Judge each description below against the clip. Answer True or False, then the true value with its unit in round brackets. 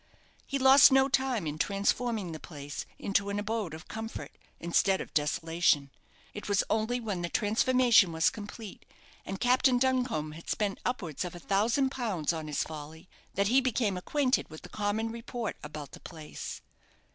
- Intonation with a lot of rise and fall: True (6.7 semitones)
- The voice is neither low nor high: False (205 Hz)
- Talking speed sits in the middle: True (170 wpm)